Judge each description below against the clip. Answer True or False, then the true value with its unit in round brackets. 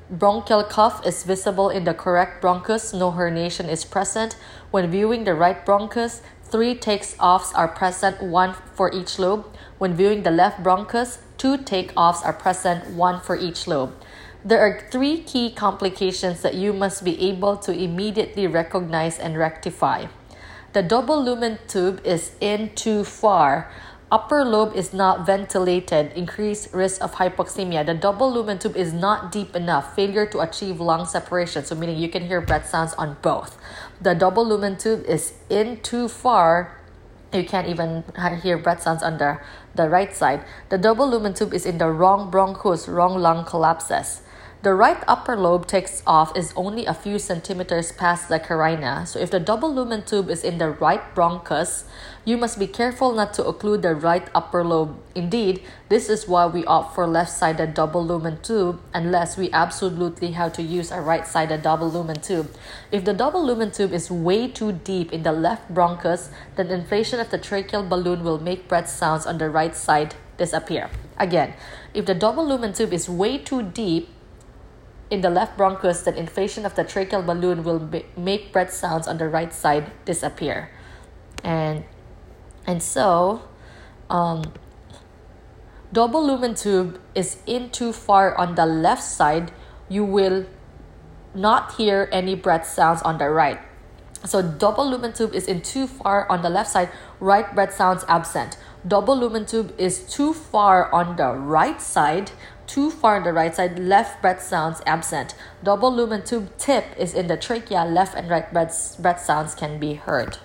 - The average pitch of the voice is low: False (185 Hz)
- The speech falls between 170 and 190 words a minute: True (175 wpm)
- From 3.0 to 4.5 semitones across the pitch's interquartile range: True (3.6 semitones)